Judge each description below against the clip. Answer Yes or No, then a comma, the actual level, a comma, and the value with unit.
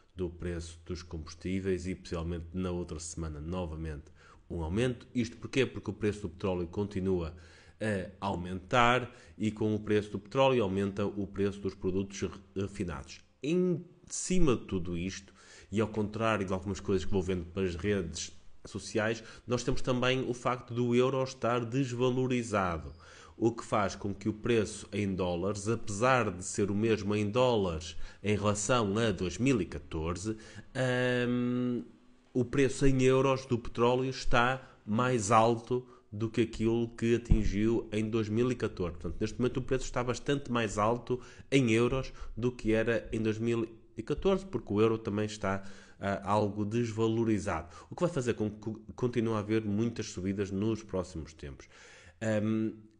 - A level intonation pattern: No, average, 4.1 semitones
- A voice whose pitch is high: No, low, 110 Hz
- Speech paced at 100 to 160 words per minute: Yes, average, 155 wpm